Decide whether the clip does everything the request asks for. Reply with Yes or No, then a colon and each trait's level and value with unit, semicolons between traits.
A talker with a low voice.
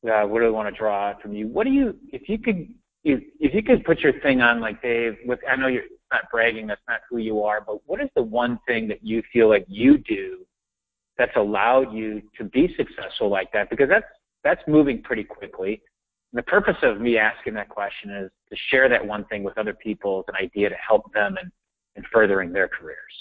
Yes: low, 115 Hz